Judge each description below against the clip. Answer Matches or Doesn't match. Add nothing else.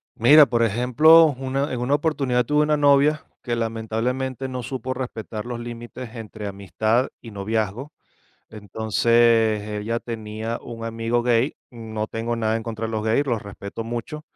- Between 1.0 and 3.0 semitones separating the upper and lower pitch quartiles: Matches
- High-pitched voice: Doesn't match